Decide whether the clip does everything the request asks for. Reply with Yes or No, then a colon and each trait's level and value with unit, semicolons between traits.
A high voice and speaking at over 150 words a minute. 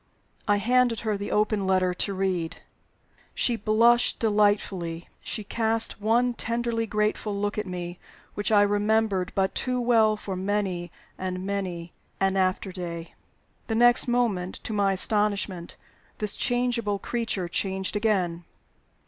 No: high, 205 Hz; slow, 135 wpm